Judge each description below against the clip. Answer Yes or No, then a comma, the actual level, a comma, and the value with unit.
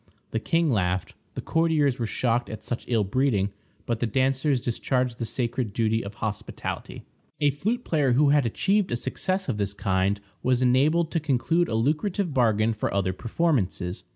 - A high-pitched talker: No, low, 125 Hz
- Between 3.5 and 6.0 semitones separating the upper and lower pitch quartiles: Yes, average, 5.3 semitones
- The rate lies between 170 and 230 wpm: Yes, average, 175 wpm